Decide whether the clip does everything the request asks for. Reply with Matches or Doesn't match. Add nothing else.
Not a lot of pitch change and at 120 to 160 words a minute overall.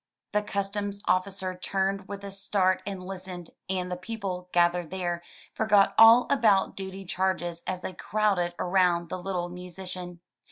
Matches